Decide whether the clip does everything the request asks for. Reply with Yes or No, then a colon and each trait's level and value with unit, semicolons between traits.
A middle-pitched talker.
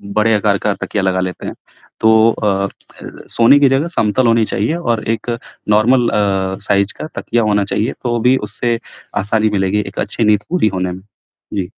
No: low, 110 Hz